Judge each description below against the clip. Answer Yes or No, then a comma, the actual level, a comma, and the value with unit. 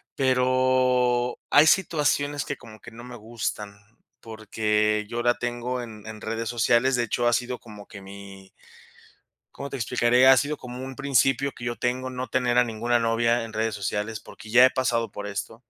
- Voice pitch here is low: Yes, low, 120 Hz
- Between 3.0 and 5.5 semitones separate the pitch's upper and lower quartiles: No, narrow, 2.6 semitones